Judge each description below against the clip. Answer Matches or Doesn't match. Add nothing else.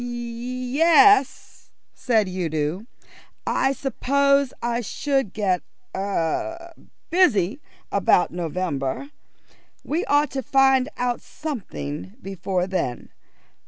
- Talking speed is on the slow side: Matches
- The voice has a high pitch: Matches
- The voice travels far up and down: Matches